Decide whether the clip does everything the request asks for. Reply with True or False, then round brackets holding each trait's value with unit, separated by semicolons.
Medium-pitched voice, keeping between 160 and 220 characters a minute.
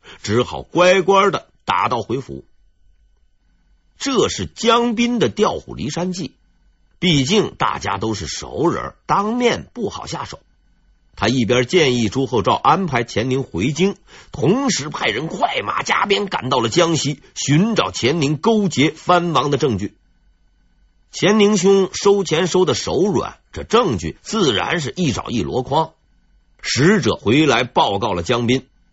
True (160 Hz; 205 characters per minute)